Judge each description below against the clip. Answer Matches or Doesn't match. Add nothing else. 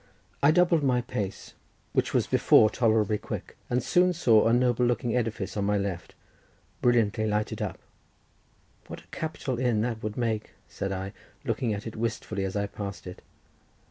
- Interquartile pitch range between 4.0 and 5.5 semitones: Doesn't match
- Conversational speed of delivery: Matches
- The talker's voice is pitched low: Matches